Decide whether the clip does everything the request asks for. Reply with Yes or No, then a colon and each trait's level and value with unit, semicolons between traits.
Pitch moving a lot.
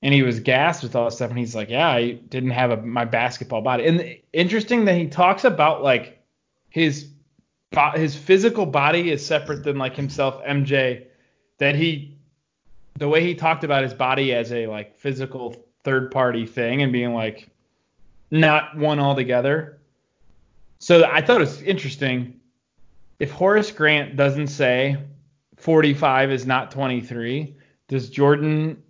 No: average, 3.5 semitones